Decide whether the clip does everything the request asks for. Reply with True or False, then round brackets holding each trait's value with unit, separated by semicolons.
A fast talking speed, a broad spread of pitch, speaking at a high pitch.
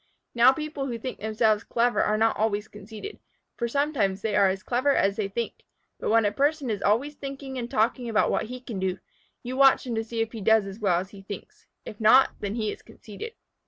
False (230 wpm; 3.7 semitones; 225 Hz)